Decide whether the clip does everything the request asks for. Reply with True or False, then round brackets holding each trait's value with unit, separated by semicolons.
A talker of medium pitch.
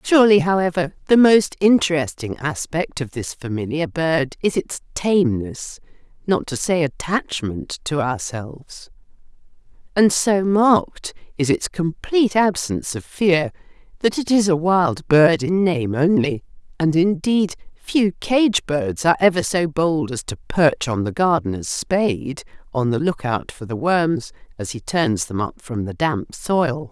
True (160 Hz)